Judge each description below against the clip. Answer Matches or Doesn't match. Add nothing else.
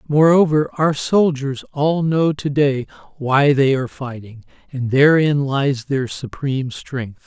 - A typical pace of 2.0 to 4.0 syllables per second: Matches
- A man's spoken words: Matches